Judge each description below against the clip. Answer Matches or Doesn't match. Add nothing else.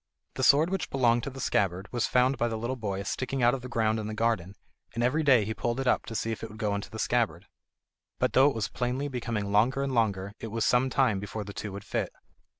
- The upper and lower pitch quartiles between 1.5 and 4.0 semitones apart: Matches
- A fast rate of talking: Matches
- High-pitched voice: Doesn't match